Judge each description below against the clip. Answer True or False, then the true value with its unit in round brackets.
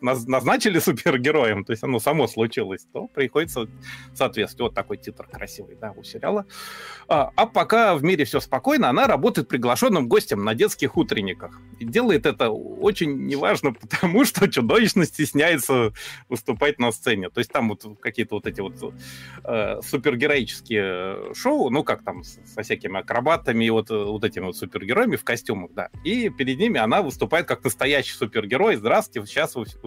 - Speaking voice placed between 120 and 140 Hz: True (135 Hz)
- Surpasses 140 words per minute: True (160 wpm)